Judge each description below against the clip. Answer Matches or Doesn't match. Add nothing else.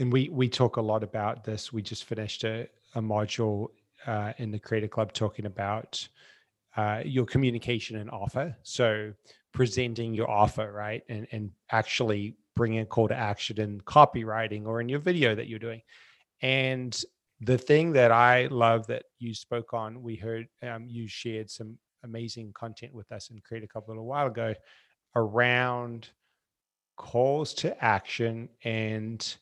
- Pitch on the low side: Matches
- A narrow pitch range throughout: Matches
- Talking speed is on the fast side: Doesn't match